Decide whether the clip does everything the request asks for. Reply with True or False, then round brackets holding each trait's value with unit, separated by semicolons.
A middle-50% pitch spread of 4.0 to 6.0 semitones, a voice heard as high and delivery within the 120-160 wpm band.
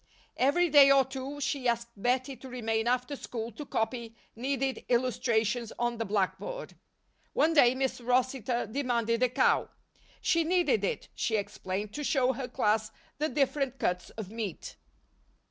False (3.3 semitones; 250 Hz; 150 wpm)